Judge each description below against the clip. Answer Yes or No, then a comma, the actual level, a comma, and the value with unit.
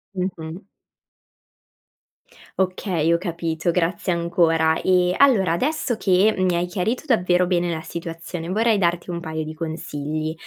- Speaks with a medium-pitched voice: Yes, medium, 175 Hz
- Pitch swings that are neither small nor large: No, narrow, 2.3 semitones